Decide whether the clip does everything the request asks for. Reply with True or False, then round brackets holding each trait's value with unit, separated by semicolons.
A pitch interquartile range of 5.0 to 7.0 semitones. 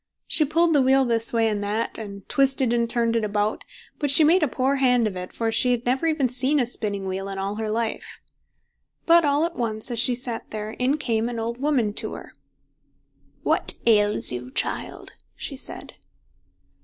False (3.8 semitones)